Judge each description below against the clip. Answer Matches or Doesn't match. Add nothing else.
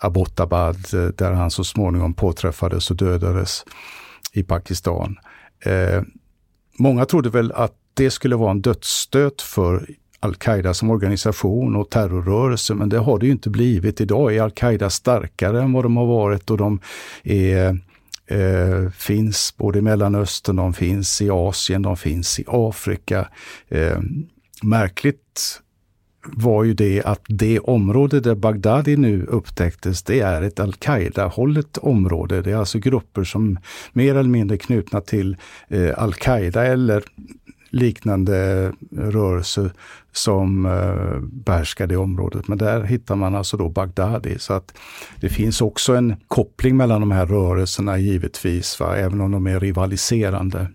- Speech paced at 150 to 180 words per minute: Doesn't match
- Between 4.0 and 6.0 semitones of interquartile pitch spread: Doesn't match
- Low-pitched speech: Matches